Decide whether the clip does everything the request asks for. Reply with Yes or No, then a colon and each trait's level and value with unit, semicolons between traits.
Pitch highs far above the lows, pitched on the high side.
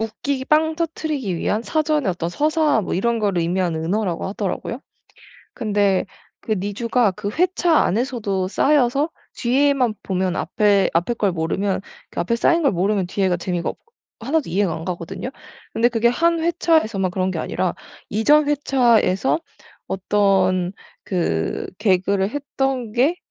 Yes: wide, 6.5 semitones; high, 215 Hz